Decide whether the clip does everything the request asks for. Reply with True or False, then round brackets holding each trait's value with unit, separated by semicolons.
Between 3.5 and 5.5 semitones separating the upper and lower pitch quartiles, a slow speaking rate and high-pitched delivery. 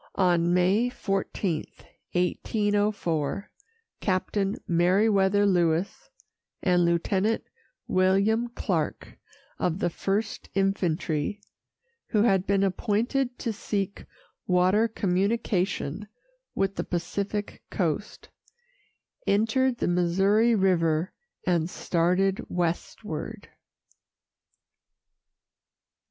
False (2.8 semitones; 80 wpm; 195 Hz)